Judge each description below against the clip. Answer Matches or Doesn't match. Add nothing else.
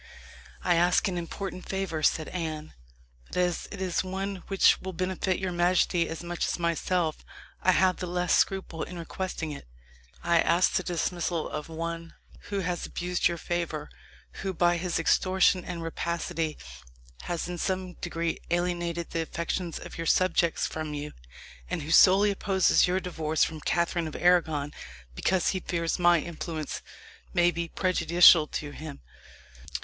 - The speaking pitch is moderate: Matches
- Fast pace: Doesn't match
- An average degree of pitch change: Doesn't match